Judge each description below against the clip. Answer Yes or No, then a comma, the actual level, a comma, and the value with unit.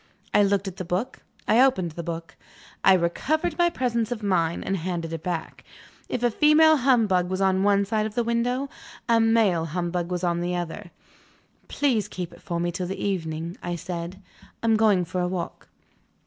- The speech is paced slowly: No, average, 195 wpm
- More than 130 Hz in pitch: Yes, high, 190 Hz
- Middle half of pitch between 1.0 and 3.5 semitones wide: No, average, 4.6 semitones